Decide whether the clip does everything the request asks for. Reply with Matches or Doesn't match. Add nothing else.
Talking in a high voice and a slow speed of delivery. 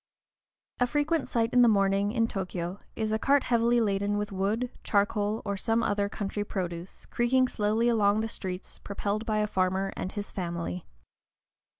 Doesn't match